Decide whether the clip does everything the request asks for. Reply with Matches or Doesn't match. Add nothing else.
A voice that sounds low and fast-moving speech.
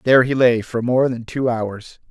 Matches